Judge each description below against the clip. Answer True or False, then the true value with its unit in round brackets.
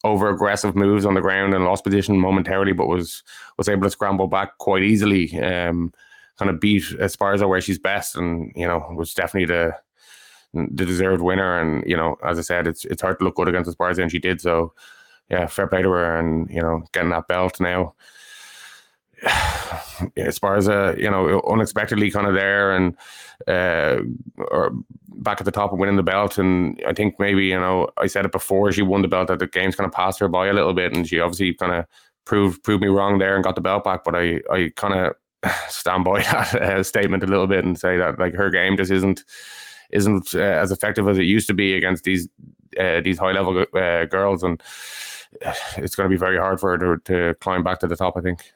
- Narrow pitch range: True (1.9 semitones)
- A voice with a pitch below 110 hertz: True (95 Hz)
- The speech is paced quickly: True (225 wpm)